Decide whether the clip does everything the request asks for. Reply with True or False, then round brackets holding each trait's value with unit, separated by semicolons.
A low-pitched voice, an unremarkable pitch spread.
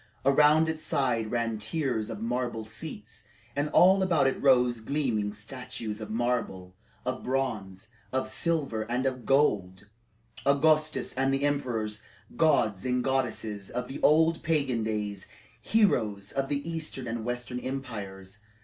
True (125 Hz; 4.4 semitones)